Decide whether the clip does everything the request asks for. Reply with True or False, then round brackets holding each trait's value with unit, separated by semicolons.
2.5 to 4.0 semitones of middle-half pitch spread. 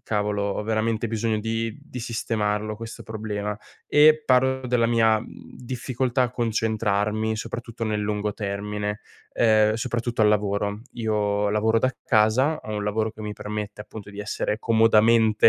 False (1.8 semitones)